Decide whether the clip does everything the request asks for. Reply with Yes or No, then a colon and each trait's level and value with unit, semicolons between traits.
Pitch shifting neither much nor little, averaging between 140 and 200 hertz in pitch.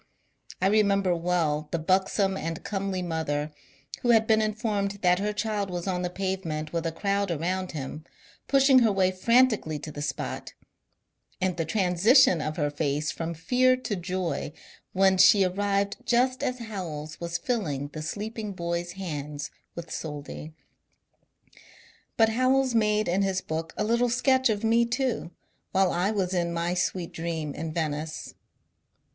Yes: average, 4.6 semitones; medium, 185 Hz